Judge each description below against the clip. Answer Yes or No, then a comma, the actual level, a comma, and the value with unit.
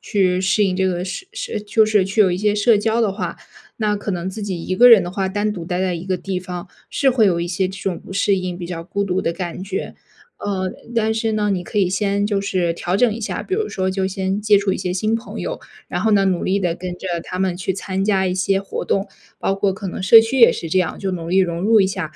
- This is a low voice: No, high, 195 Hz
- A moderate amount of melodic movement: No, narrow, 2.2 semitones